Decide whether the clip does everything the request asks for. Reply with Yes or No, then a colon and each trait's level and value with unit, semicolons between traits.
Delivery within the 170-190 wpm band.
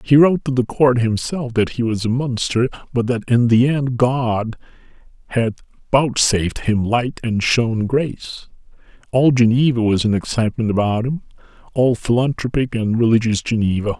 No: average, 150 wpm